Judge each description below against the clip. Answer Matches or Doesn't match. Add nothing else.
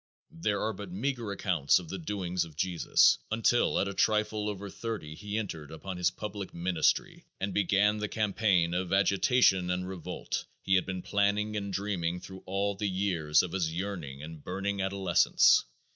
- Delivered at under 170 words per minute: Doesn't match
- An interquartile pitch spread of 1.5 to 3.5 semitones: Matches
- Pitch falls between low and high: Doesn't match